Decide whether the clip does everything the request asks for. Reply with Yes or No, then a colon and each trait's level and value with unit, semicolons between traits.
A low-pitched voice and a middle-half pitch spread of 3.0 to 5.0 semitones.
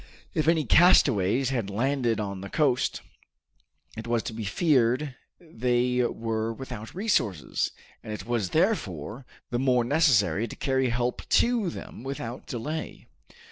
Yes: low, 125 Hz; average, 4.2 semitones